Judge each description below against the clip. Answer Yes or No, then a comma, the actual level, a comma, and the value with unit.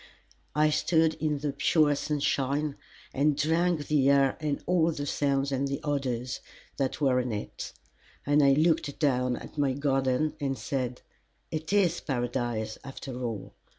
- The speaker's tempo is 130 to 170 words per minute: Yes, average, 150 wpm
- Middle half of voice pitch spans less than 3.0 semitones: Yes, narrow, 2.6 semitones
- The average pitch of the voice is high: No, medium, 140 Hz